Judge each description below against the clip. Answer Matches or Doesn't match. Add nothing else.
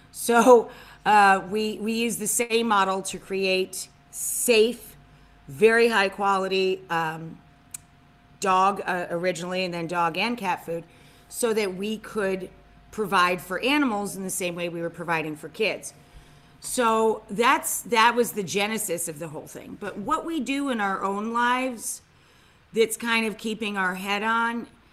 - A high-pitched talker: Matches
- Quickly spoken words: Doesn't match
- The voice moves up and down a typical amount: Matches